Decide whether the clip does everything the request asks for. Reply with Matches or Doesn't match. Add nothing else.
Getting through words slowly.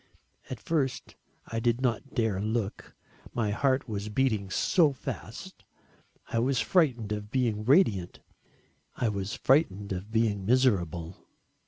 Matches